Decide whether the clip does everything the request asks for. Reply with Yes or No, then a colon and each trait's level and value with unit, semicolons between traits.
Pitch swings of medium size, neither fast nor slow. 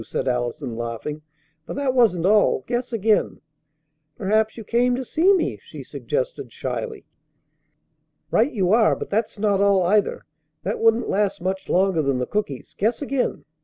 Yes: average, 5.0 semitones; average, 160 wpm